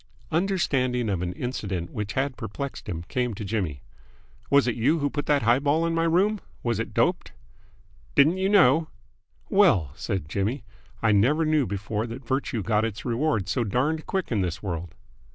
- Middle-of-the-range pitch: No, low, 125 Hz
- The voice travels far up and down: Yes, wide, 7.0 semitones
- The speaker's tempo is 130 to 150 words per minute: No, average, 180 wpm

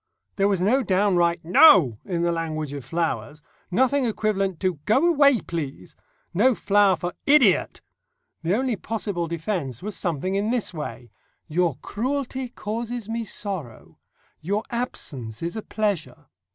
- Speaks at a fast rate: No, average, 140 wpm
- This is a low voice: No, high, 190 Hz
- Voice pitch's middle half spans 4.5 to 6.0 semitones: Yes, average, 5.3 semitones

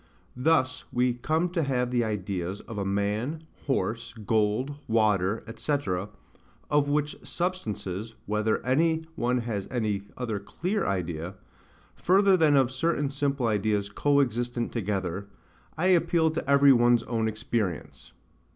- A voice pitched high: No, low, 120 Hz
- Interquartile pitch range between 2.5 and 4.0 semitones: No, wide, 5.6 semitones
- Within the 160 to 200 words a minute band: No, slow, 135 wpm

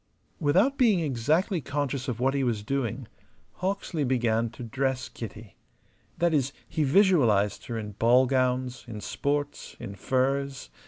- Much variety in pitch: No, average, 3.8 semitones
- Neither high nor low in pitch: No, low, 130 Hz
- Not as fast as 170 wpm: Yes, average, 145 wpm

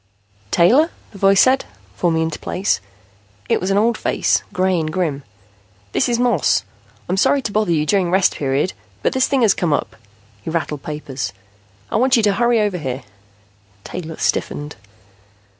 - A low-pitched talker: No, medium, 185 Hz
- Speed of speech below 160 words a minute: No, average, 170 wpm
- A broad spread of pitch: Yes, wide, 5.8 semitones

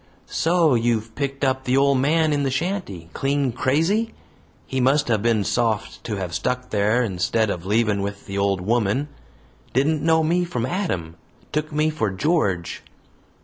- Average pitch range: No, wide, 6.6 semitones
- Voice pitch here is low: Yes, low, 125 Hz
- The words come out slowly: No, average, 165 wpm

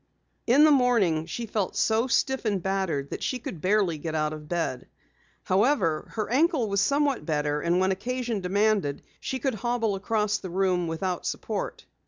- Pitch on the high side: Yes, high, 200 Hz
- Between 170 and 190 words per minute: Yes, average, 175 wpm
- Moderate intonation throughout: No, wide, 5.8 semitones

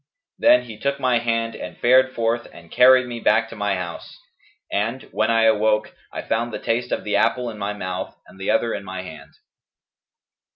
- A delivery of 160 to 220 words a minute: Yes, average, 200 wpm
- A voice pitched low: Yes, low, 115 Hz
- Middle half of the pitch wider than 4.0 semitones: No, average, 2.8 semitones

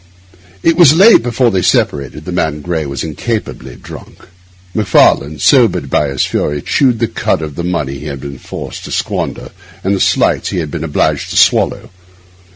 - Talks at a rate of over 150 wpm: Yes, average, 180 wpm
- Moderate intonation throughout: No, wide, 7.8 semitones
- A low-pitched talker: Yes, very low, 80 Hz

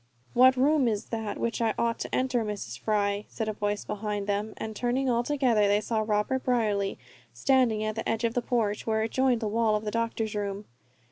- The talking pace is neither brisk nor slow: No, fast, 215 wpm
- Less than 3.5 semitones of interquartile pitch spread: Yes, narrow, 2.5 semitones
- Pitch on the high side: Yes, high, 220 Hz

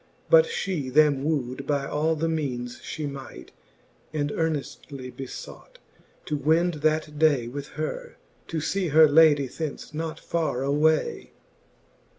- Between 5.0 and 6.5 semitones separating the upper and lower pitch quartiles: No, narrow, 2.5 semitones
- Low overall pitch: No, medium, 150 Hz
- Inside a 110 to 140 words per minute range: Yes, slow, 135 wpm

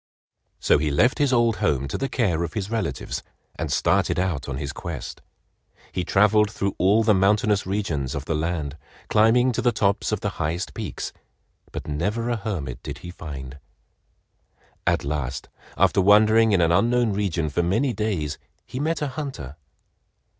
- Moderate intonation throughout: No, wide, 6.4 semitones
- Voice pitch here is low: Yes, low, 100 Hz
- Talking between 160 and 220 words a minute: Yes, average, 170 wpm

